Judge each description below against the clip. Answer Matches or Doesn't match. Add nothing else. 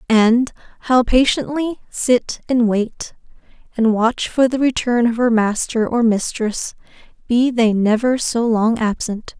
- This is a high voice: Matches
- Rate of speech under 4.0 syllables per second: Matches